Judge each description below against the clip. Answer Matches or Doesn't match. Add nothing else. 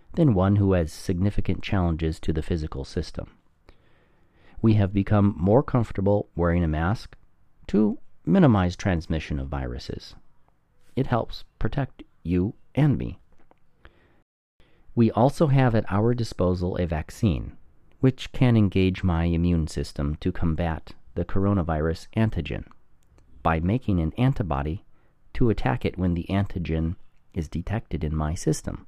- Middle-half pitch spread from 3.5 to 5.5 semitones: Matches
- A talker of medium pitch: Doesn't match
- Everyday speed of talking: Doesn't match